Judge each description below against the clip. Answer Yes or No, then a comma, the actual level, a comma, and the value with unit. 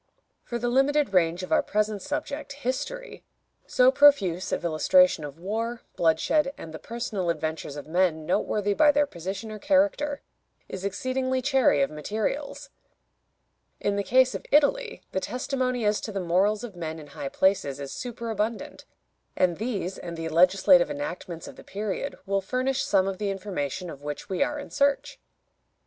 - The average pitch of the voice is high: Yes, high, 205 Hz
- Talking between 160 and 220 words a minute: Yes, average, 165 wpm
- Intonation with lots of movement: Yes, wide, 6.8 semitones